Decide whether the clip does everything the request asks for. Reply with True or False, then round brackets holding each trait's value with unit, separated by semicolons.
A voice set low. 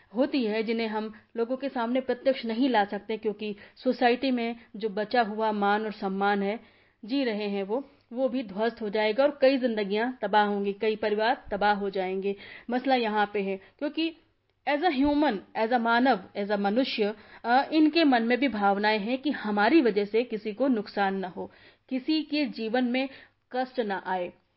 False (225 Hz)